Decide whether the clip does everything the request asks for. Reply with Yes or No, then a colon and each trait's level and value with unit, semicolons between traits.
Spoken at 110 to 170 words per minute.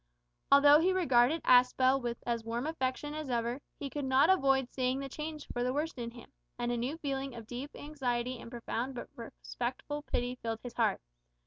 No: average, 195 wpm